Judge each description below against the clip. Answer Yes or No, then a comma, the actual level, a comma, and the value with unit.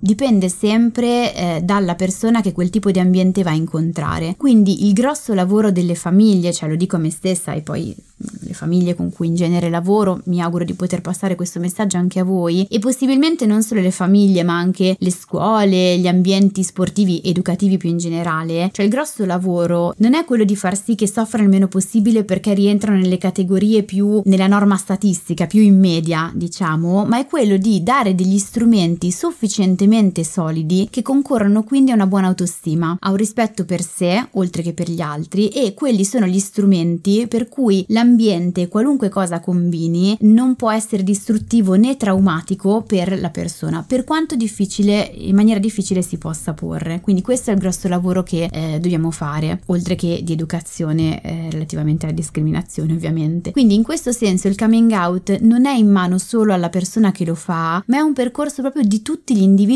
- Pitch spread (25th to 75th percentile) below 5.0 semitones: Yes, average, 3.6 semitones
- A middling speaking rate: No, fast, 190 wpm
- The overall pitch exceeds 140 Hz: Yes, high, 190 Hz